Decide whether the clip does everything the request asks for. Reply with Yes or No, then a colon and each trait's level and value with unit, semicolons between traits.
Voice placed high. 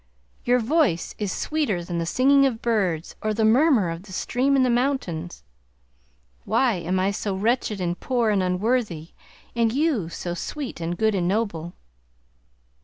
Yes: high, 215 Hz